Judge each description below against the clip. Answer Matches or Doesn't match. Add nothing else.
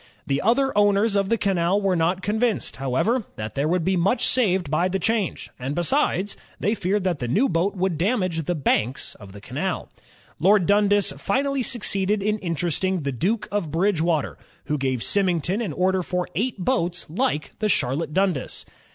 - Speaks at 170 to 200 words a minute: Matches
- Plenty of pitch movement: Doesn't match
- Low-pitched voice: Doesn't match